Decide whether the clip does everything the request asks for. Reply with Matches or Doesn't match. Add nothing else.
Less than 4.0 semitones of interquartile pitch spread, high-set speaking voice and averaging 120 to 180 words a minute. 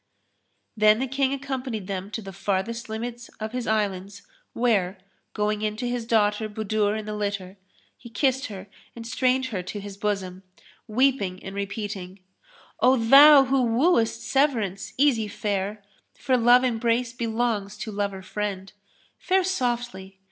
Matches